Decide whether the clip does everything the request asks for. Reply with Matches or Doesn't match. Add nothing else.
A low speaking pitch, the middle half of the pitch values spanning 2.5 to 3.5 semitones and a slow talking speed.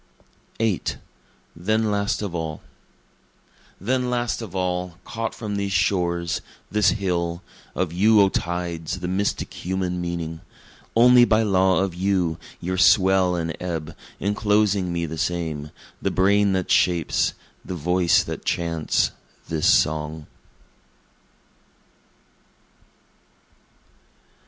Matches